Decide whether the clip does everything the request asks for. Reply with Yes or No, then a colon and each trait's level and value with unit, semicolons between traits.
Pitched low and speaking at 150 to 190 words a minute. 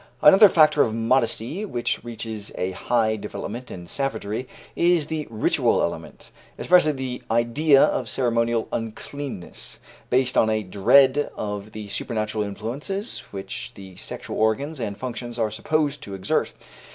No: low, 115 Hz; average, 140 wpm